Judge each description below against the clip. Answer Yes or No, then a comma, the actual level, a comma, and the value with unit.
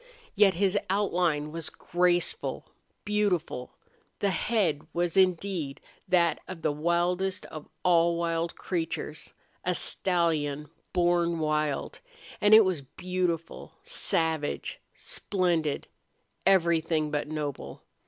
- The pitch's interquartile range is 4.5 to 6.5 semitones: No, average, 2.9 semitones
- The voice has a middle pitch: Yes, medium, 170 Hz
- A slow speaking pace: Yes, slow, 105 wpm